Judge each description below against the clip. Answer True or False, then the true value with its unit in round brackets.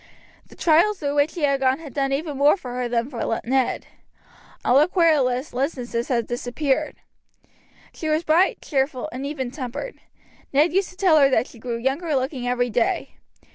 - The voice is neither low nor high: False (275 Hz)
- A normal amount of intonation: True (3.8 semitones)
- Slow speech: False (180 wpm)